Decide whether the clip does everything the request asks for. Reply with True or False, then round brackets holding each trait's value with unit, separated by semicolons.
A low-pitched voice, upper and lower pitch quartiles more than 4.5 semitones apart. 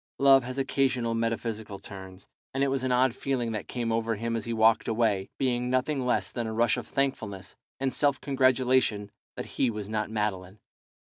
False (115 Hz; 3.3 semitones)